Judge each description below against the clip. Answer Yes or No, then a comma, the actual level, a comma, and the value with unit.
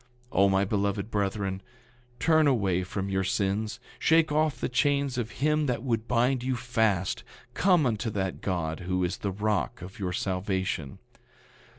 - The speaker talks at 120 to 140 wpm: No, average, 165 wpm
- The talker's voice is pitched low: Yes, low, 105 Hz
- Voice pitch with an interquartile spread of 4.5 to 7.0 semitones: Yes, average, 4.8 semitones